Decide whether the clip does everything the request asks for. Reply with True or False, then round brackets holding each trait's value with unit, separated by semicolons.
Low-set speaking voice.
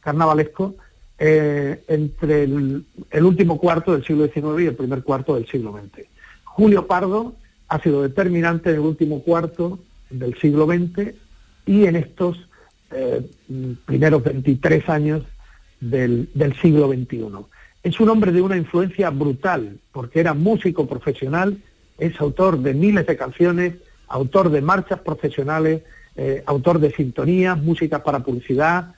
False (155 Hz)